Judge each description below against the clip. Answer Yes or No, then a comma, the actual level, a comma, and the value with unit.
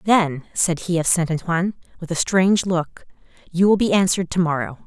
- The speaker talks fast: No, average, 195 wpm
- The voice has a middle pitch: Yes, medium, 175 Hz